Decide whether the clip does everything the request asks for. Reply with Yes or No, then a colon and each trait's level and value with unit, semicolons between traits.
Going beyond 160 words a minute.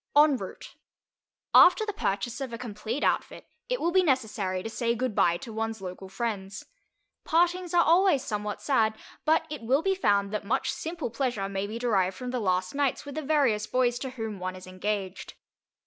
Yes: average, 190 wpm